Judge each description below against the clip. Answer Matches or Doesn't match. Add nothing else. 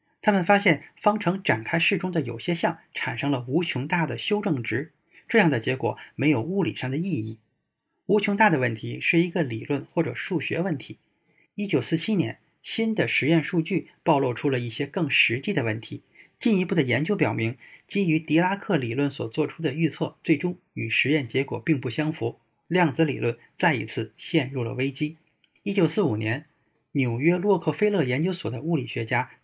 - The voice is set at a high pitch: Doesn't match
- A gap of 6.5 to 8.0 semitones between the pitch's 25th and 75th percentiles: Doesn't match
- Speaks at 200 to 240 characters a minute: Doesn't match